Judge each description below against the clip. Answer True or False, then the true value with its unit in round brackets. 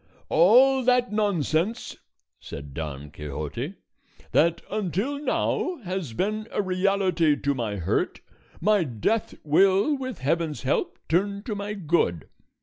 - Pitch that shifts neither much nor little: False (6.8 semitones)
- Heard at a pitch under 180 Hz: False (185 Hz)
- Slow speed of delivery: True (125 wpm)